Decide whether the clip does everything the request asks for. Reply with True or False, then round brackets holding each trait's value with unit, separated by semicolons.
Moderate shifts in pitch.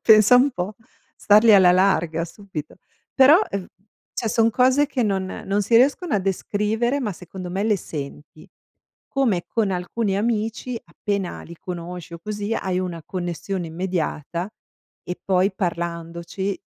True (3.9 semitones)